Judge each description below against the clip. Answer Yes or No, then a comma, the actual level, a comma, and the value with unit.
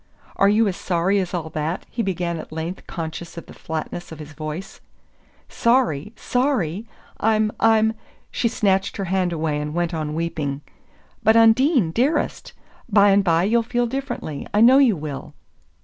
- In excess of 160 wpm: Yes, average, 170 wpm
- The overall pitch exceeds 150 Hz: Yes, high, 190 Hz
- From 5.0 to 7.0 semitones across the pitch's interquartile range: Yes, wide, 5.6 semitones